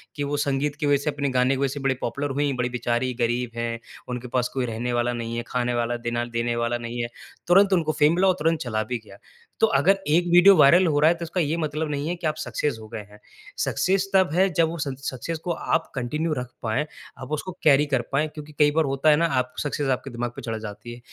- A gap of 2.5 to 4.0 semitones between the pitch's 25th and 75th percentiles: No, average, 4.5 semitones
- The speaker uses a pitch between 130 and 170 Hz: Yes, medium, 140 Hz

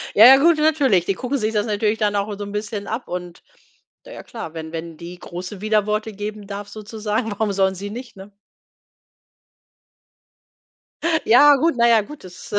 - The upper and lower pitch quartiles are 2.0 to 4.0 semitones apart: Yes, average, 2.9 semitones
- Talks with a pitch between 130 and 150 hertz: No, high, 210 Hz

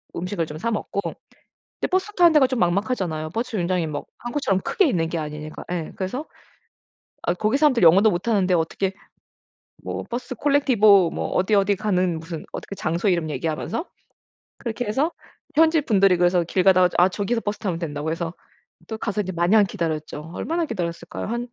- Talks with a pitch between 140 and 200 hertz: Yes, high, 190 Hz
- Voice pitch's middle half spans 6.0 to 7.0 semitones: No, wide, 5.4 semitones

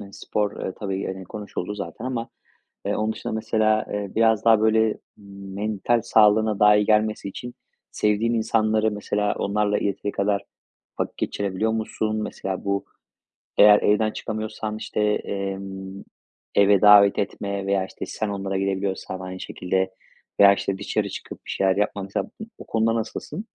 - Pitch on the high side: No, low, 105 Hz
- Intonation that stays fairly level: Yes, narrow, 1.8 semitones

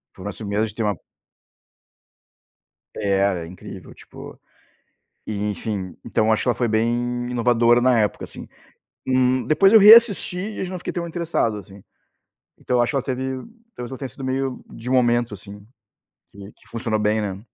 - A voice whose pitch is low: Yes, low, 120 Hz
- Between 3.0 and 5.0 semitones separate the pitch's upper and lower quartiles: Yes, average, 3.8 semitones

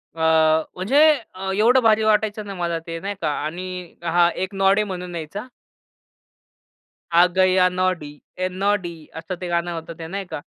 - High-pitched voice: No, medium, 180 Hz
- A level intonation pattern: No, average, 3.0 semitones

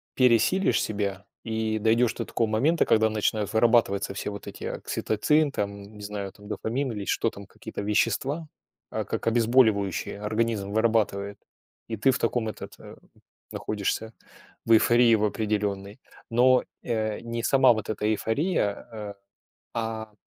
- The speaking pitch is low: Yes, low, 110 Hz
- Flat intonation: Yes, narrow, 2.2 semitones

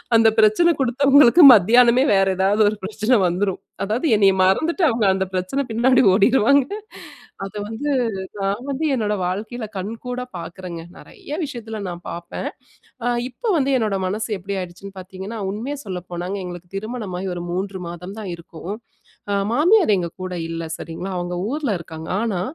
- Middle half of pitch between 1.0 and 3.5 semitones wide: No, average, 4.8 semitones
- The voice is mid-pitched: No, high, 205 Hz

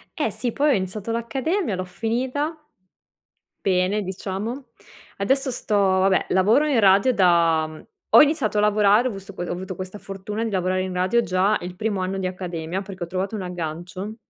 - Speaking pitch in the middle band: No, high, 195 Hz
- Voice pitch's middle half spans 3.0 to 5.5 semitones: Yes, average, 3.6 semitones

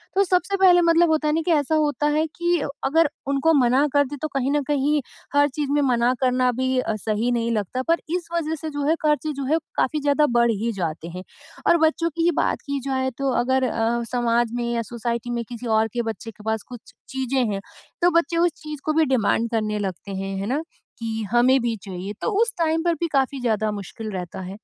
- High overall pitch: Yes, very high, 260 Hz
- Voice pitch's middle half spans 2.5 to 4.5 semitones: No, average, 5.2 semitones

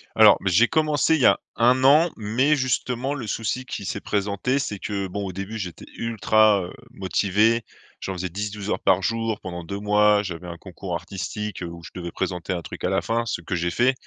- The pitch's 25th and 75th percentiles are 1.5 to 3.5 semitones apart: No, average, 4.0 semitones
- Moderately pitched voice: No, low, 105 Hz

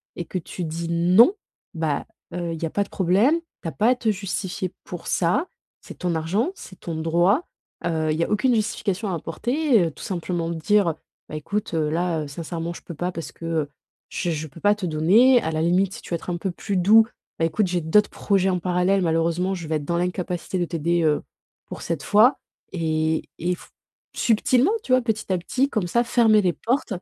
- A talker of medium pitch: Yes, medium, 180 Hz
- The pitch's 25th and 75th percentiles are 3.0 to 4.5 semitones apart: Yes, average, 4.1 semitones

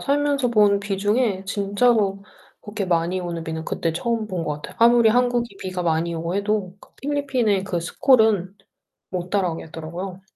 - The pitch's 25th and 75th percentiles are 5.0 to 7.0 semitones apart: No, average, 4.6 semitones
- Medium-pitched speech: No, high, 200 Hz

